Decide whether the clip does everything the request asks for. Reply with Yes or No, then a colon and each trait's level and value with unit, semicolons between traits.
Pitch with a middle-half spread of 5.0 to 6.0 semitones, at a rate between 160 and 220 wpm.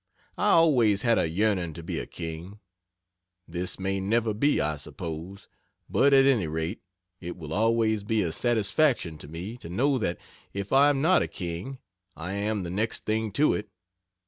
Yes: average, 5.3 semitones; average, 180 wpm